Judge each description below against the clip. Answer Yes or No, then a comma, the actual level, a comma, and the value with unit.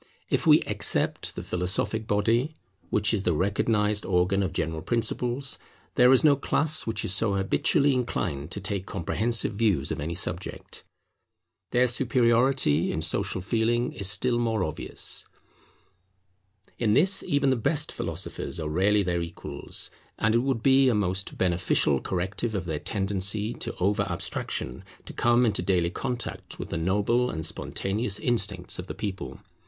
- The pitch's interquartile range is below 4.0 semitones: No, average, 4.5 semitones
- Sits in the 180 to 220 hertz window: No, low, 105 Hz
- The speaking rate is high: No, average, 155 wpm